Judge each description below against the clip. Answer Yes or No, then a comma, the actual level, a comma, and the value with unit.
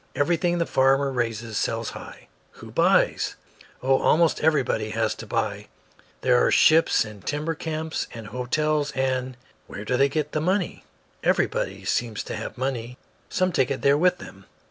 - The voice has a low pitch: Yes, low, 130 Hz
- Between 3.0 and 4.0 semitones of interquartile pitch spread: No, average, 5.1 semitones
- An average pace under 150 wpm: No, average, 170 wpm